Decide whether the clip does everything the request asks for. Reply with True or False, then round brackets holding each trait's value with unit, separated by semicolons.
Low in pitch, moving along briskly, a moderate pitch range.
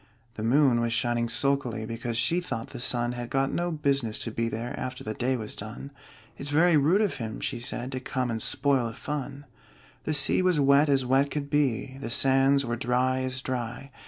True (130 Hz; 210 wpm; 3.0 semitones)